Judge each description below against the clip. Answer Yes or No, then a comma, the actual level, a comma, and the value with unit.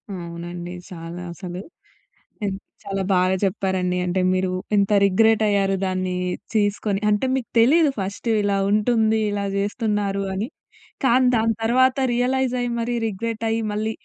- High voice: Yes, high, 205 Hz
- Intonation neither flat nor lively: Yes, average, 3.4 semitones